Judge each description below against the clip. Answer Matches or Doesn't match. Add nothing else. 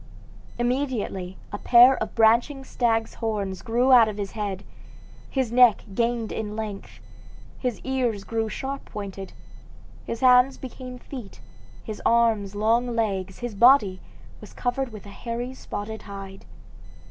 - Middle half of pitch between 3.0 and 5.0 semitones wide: Matches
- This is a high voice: Matches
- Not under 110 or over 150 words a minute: Matches